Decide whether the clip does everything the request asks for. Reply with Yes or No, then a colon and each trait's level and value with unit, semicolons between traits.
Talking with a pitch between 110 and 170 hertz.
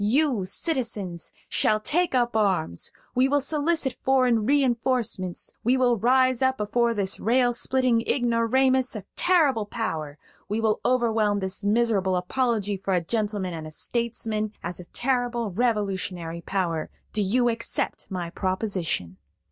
No: high, 225 Hz